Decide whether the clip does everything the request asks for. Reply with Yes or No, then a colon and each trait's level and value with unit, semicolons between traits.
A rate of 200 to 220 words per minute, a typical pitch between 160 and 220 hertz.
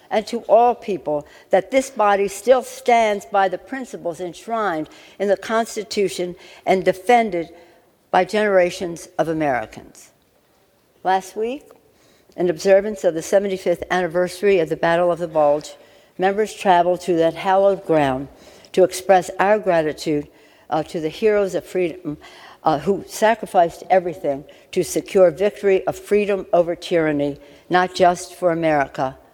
No: slow, 135 wpm; medium, 185 Hz